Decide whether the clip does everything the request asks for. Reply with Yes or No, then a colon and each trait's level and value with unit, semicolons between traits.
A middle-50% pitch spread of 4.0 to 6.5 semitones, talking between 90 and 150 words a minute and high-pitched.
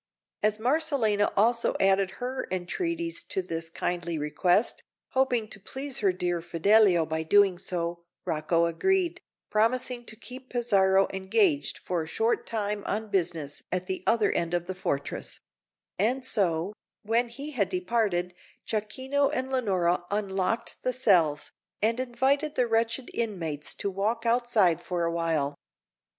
Yes: wide, 5.5 semitones; average, 140 wpm; high, 205 Hz